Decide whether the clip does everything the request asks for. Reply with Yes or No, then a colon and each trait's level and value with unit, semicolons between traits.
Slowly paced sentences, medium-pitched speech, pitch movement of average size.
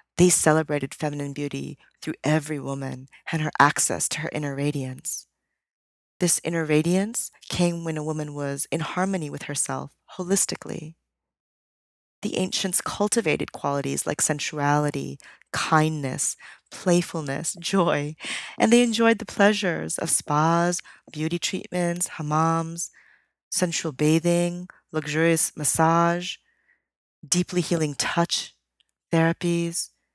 Yes: slow, 105 wpm; medium, 165 Hz; average, 3.2 semitones